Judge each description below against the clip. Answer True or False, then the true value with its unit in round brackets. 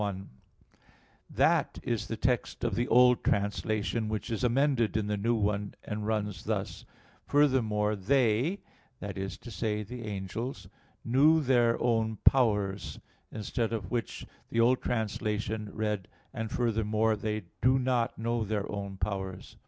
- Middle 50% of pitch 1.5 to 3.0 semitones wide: True (2.5 semitones)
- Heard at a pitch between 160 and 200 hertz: False (110 Hz)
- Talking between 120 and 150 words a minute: True (145 wpm)